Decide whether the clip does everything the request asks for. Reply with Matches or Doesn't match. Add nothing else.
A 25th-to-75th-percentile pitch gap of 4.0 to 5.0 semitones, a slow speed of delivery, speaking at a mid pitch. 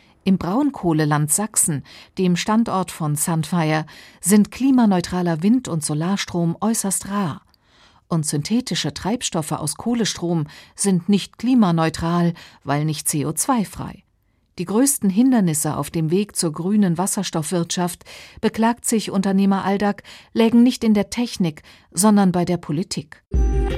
Matches